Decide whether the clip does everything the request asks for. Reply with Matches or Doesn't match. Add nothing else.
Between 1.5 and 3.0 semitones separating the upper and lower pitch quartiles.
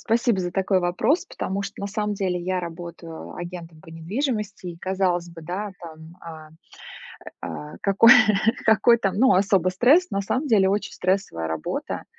Doesn't match